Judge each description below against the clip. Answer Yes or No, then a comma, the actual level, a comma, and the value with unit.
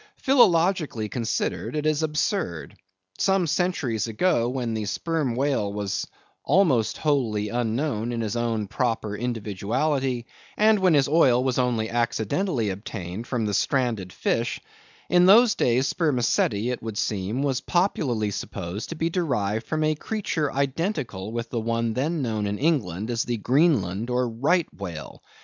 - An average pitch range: No, wide, 5.9 semitones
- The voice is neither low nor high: No, low, 120 Hz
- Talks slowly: No, average, 150 wpm